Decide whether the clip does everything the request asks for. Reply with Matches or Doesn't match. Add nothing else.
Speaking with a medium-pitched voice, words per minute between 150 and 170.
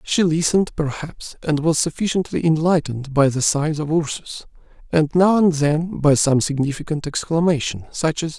Matches